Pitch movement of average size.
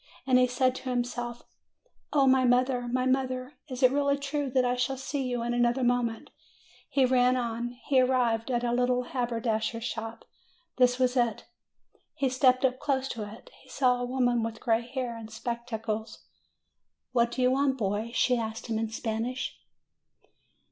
No: narrow, 1.6 semitones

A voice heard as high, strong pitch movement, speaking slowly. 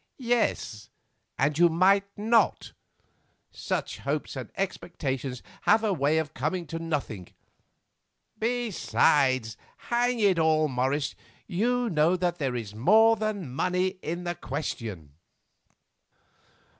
No: medium, 170 Hz; wide, 6.9 semitones; slow, 115 wpm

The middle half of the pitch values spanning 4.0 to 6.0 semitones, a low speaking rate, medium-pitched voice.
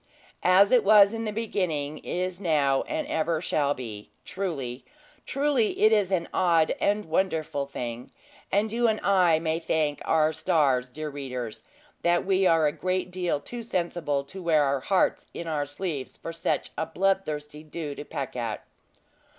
No: average, 4.8 semitones; average, 165 wpm; medium, 165 Hz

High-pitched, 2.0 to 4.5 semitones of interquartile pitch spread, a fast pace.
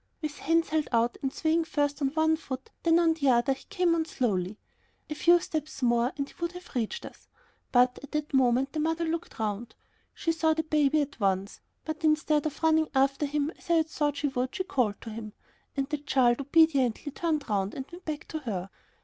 Yes: very high, 290 Hz; average, 4.1 semitones; fast, 220 wpm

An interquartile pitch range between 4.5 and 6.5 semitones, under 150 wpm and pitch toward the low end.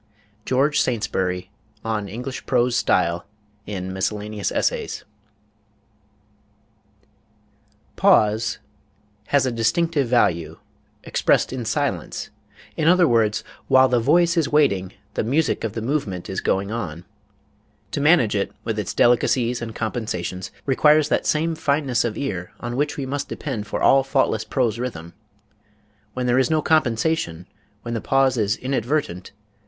Yes: average, 5.2 semitones; slow, 135 wpm; low, 120 Hz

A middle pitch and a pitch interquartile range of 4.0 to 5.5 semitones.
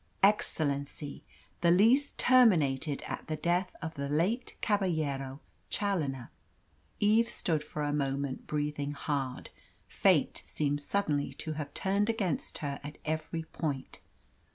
Yes: medium, 155 Hz; average, 5.1 semitones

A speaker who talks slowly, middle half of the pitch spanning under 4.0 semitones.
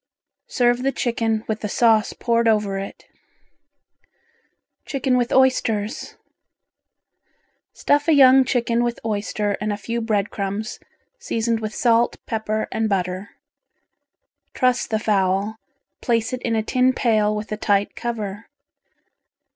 Yes: slow, 130 wpm; narrow, 2.4 semitones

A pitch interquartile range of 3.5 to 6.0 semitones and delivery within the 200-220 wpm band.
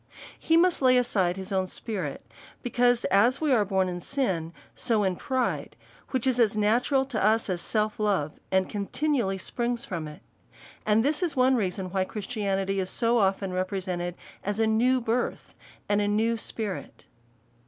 No: average, 4.4 semitones; average, 170 wpm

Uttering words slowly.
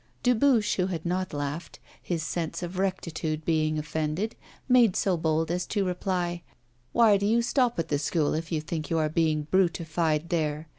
No: average, 180 wpm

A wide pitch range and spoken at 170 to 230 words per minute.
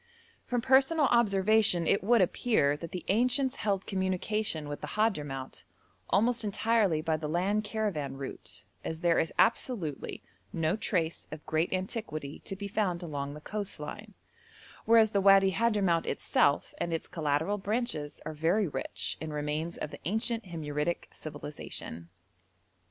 No: wide, 5.7 semitones; average, 145 wpm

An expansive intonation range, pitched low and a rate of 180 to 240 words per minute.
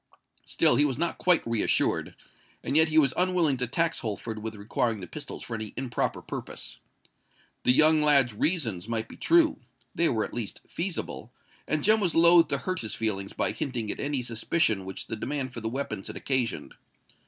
Yes: wide, 6.0 semitones; low, 130 Hz; average, 190 wpm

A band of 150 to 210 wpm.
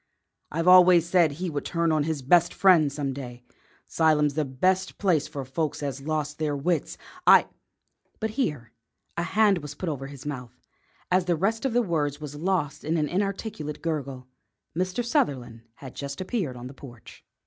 Yes: average, 185 wpm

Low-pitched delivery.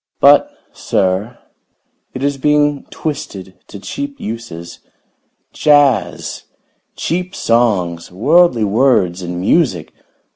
Yes: low, 120 Hz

